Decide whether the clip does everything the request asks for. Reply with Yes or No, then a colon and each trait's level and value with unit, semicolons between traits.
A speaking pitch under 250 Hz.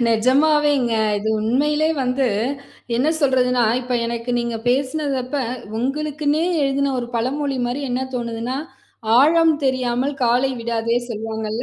No: very high, 255 Hz